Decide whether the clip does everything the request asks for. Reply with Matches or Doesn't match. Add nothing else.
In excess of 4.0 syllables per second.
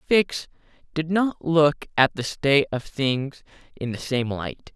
Doesn't match